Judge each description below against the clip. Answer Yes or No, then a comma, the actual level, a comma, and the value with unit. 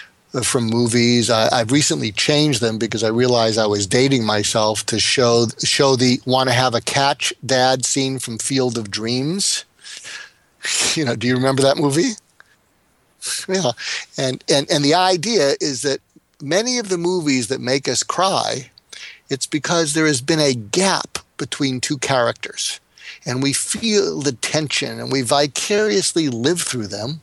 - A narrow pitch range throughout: No, average, 4.5 semitones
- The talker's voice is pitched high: No, low, 135 Hz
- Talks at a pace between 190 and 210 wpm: No, average, 160 wpm